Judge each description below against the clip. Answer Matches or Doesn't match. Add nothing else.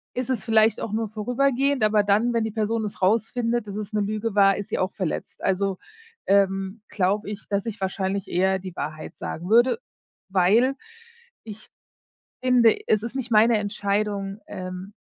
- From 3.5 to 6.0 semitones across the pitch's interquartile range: Doesn't match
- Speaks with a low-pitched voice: Doesn't match